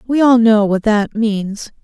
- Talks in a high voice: Yes, high, 220 Hz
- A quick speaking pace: No, average, 195 wpm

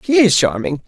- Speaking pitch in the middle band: Yes, medium, 180 Hz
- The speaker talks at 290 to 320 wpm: No, fast, 205 wpm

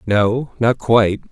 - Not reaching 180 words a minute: Yes, slow, 135 wpm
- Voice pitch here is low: Yes, low, 115 Hz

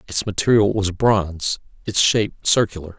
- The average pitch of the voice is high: No, low, 100 Hz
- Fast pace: No, average, 140 wpm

